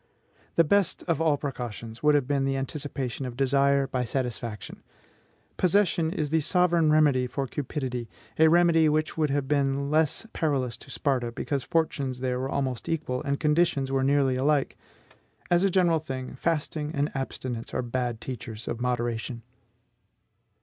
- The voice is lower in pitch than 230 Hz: Yes, medium, 140 Hz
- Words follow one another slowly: No, average, 160 wpm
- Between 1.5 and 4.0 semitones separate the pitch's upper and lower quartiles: Yes, average, 3.5 semitones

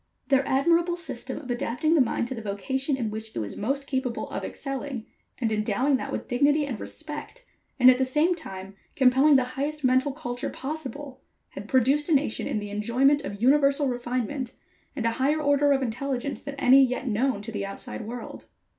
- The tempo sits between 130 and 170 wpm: No, average, 190 wpm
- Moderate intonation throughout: Yes, average, 3.4 semitones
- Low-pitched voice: No, very high, 265 Hz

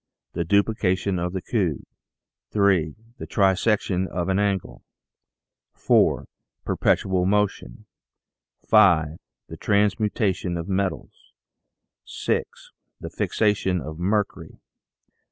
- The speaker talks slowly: Yes, slow, 100 wpm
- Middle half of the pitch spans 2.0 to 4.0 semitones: Yes, average, 2.7 semitones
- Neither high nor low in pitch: No, very low, 95 Hz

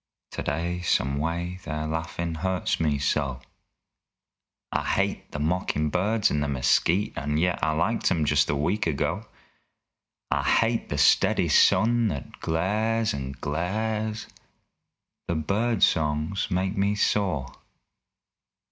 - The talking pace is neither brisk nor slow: No, slow, 130 wpm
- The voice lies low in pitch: Yes, very low, 85 Hz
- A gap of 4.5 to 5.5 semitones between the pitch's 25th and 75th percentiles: Yes, average, 5.1 semitones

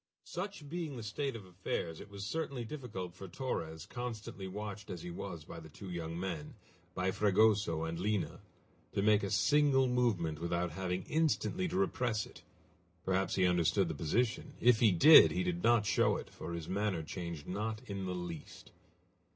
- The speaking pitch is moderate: No, low, 100 Hz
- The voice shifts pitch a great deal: Yes, wide, 5.8 semitones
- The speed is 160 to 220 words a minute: Yes, average, 180 wpm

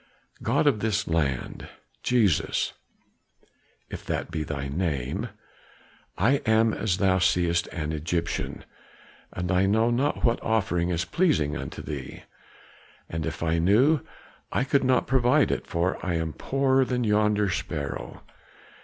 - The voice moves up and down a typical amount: No, wide, 6.2 semitones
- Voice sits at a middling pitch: No, very low, 95 Hz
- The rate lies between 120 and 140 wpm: Yes, slow, 135 wpm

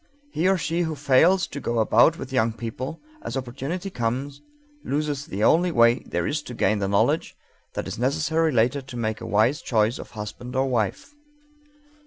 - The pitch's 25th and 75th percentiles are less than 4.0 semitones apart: No, average, 4.9 semitones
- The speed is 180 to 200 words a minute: Yes, average, 185 wpm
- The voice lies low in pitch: Yes, low, 130 Hz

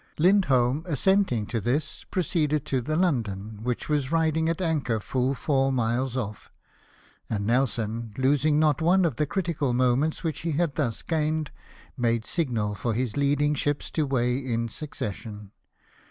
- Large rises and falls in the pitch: No, average, 4.8 semitones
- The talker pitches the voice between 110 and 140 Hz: Yes, low, 135 Hz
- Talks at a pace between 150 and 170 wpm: Yes, average, 155 wpm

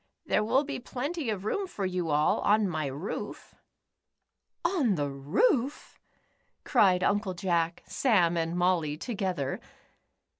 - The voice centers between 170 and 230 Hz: Yes, medium, 185 Hz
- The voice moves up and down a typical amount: No, wide, 6.2 semitones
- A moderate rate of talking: No, slow, 125 wpm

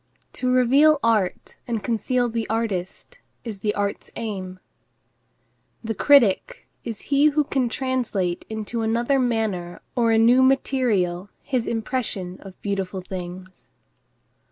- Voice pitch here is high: Yes, high, 225 Hz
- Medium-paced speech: No, slow, 120 wpm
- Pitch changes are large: No, average, 4.7 semitones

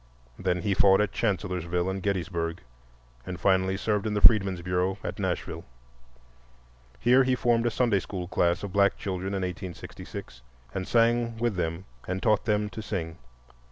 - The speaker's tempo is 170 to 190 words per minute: No, average, 160 wpm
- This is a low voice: Yes, very low, 95 Hz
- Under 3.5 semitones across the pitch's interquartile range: Yes, average, 2.9 semitones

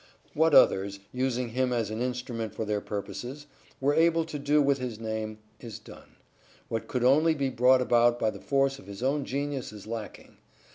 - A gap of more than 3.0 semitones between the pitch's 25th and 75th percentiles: Yes, average, 3.8 semitones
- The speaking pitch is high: No, low, 125 Hz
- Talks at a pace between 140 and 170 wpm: No, average, 190 wpm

